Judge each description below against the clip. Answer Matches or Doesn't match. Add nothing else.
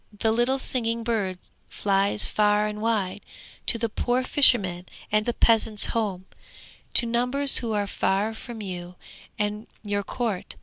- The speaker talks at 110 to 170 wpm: Matches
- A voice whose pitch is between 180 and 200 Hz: Doesn't match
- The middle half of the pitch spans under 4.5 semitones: Matches